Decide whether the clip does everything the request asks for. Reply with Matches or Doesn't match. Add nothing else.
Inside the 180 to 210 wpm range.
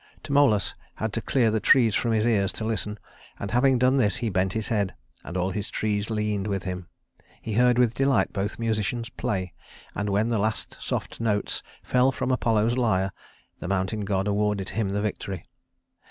Matches